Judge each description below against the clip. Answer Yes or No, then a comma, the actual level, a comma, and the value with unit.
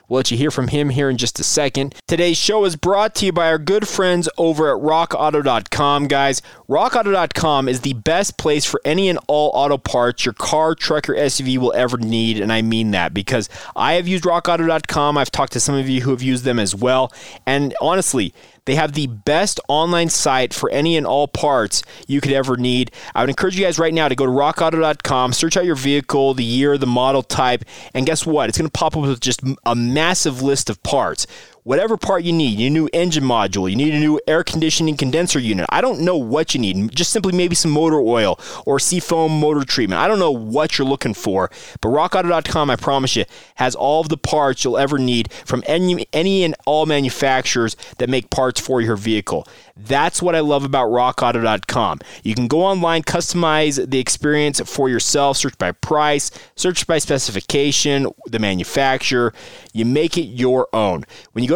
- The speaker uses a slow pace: No, fast, 205 wpm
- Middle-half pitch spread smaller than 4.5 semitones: Yes, average, 4.0 semitones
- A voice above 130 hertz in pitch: Yes, medium, 140 Hz